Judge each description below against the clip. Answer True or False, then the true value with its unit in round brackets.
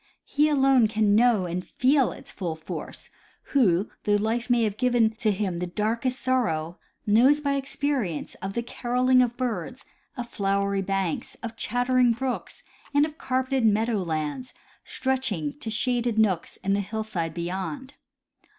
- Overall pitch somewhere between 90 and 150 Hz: False (225 Hz)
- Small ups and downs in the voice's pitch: False (4.6 semitones)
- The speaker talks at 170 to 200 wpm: False (155 wpm)